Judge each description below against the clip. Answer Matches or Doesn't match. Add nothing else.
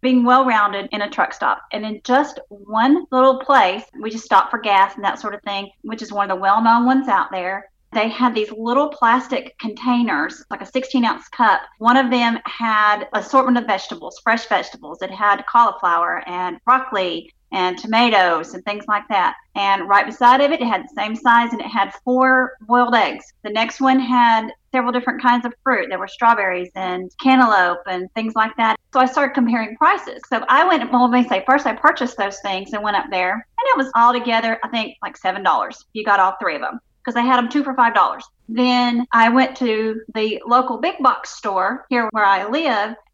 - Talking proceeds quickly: Matches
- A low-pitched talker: Doesn't match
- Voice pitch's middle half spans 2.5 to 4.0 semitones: Matches